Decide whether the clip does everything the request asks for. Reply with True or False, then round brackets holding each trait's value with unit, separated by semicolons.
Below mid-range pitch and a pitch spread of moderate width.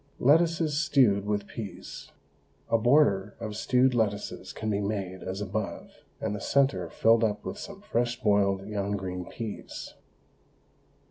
True (105 Hz; 3.8 semitones)